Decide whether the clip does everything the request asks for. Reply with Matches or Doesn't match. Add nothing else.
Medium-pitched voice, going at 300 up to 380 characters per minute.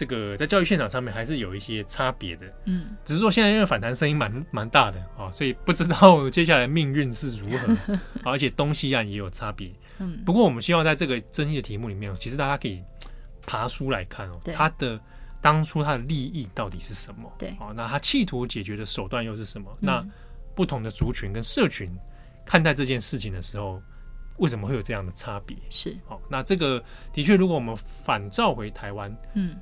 Doesn't match